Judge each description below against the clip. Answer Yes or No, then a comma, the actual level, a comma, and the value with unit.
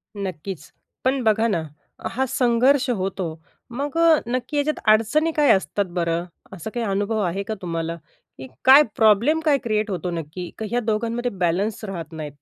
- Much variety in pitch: Yes, wide, 5.7 semitones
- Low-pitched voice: No, high, 215 Hz